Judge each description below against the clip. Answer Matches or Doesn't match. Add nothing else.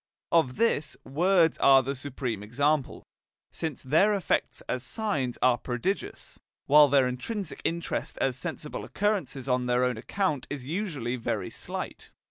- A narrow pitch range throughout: Doesn't match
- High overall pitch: Doesn't match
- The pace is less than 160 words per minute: Matches